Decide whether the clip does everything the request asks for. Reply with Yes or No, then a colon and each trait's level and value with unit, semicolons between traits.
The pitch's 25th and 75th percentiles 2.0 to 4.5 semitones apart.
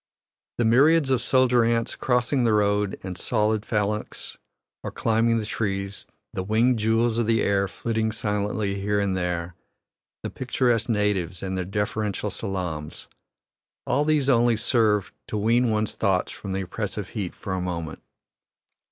Yes: average, 2.9 semitones